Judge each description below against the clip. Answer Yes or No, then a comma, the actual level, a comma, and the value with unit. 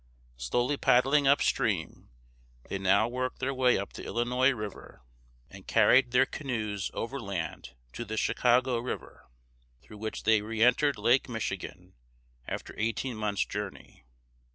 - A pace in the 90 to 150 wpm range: Yes, slow, 135 wpm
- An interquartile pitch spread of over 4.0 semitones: No, average, 3.4 semitones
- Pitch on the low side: Yes, low, 120 Hz